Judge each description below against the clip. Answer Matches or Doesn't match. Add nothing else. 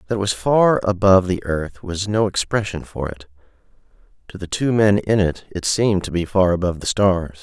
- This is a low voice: Matches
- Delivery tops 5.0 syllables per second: Matches